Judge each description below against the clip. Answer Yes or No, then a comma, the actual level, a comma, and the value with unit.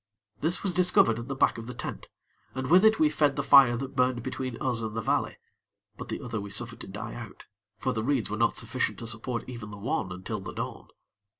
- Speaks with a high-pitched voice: No, low, 120 Hz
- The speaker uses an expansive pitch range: No, average, 3.1 semitones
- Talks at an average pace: No, fast, 235 wpm